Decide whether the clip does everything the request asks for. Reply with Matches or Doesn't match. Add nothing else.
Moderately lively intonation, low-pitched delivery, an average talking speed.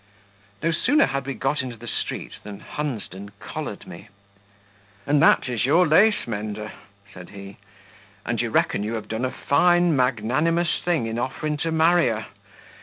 Doesn't match